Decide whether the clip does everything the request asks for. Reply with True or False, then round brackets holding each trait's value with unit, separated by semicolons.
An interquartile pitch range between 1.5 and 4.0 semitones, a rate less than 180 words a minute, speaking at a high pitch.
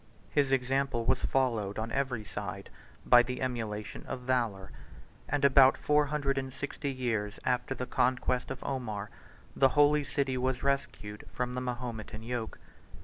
False (2.9 semitones; 150 wpm; 125 Hz)